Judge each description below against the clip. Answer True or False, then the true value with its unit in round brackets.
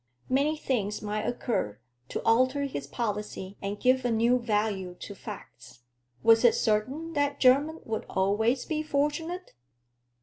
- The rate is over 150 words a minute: False (140 wpm)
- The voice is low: False (235 Hz)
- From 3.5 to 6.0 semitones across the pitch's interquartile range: True (5.2 semitones)